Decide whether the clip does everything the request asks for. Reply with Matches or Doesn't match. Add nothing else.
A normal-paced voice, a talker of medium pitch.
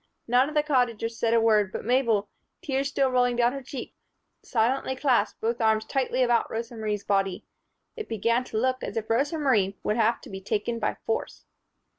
Doesn't match